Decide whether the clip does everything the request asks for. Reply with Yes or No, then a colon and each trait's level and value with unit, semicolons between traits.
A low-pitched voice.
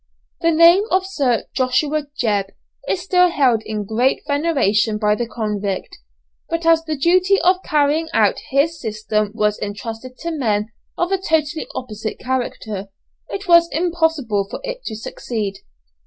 No: very high, 275 Hz